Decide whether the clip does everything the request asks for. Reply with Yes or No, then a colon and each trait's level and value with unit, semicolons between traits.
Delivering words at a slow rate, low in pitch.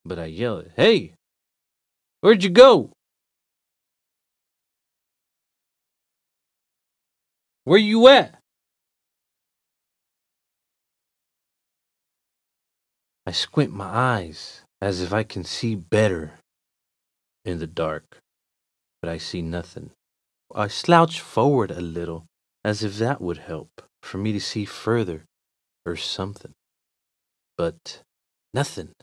Yes: slow, 95 wpm; very low, 95 Hz